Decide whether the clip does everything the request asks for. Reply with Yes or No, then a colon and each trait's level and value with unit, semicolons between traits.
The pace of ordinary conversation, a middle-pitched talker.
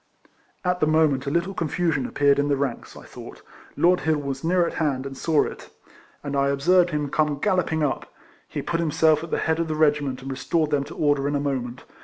No: fast, 225 wpm; medium, 150 Hz